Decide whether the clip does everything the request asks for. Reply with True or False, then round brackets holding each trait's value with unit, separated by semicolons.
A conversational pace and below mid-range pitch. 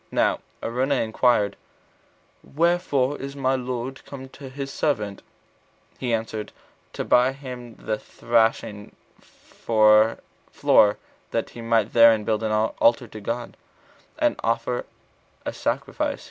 False (120 wpm; 115 Hz)